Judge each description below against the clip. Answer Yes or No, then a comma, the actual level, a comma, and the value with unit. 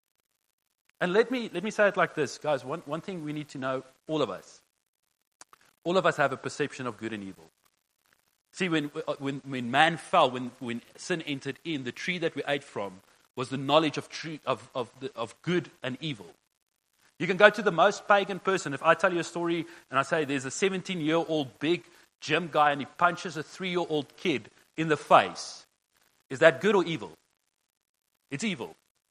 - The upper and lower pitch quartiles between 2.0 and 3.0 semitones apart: No, average, 4.4 semitones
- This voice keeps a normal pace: No, fast, 210 wpm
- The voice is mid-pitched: Yes, medium, 155 Hz